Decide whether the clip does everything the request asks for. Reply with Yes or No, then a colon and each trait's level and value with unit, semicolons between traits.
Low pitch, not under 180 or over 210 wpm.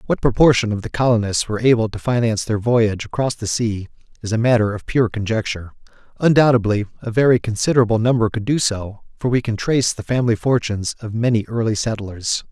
Yes: low, 115 Hz; average, 185 wpm